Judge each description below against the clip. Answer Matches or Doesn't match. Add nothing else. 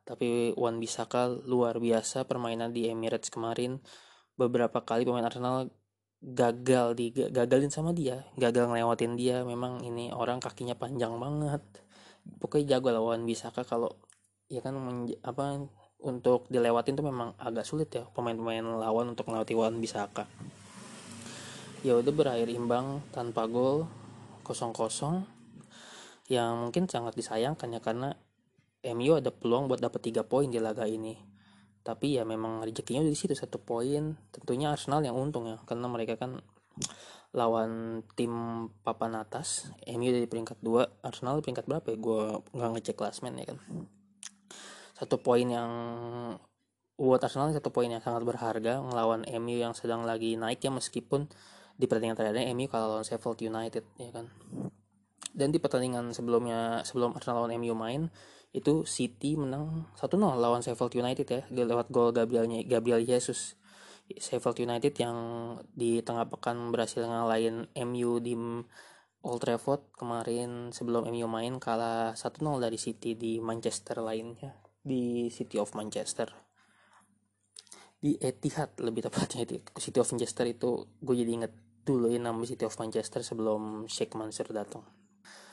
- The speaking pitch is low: Matches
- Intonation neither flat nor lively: Doesn't match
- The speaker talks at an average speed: Doesn't match